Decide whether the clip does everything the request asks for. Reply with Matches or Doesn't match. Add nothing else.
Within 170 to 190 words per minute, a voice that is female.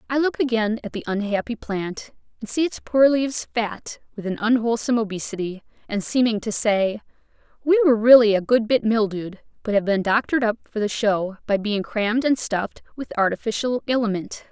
Matches